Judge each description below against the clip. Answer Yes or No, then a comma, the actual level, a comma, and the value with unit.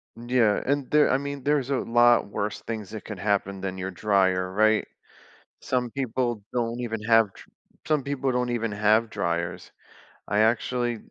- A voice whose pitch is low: Yes, low, 115 Hz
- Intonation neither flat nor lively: Yes, average, 3.4 semitones